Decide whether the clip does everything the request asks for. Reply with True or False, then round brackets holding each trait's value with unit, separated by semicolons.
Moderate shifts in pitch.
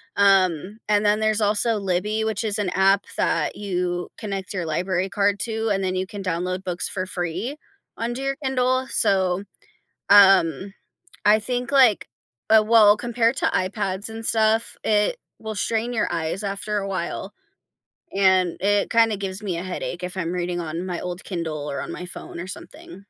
True (3.0 semitones)